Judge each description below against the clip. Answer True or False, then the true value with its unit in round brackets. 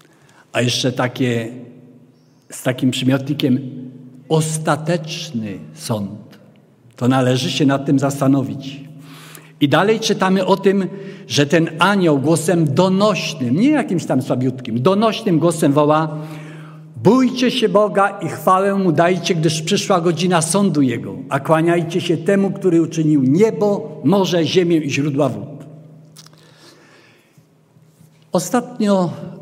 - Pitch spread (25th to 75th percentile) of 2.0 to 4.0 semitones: False (4.9 semitones)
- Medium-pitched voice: True (155 Hz)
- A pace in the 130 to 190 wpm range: False (115 wpm)